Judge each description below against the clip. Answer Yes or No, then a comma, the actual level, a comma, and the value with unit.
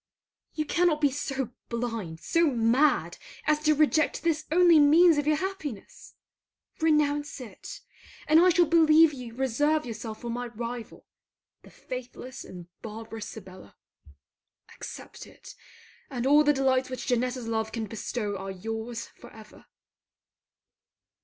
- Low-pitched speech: No, very high, 255 Hz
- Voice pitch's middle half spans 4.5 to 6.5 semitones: Yes, average, 5.1 semitones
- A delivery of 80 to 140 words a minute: Yes, slow, 135 wpm